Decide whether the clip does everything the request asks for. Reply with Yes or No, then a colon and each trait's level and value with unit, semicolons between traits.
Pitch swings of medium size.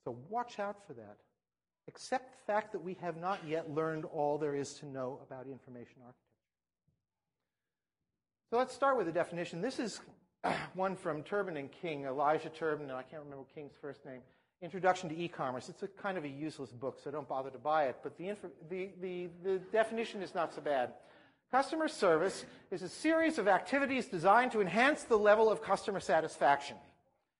No: wide, 6.1 semitones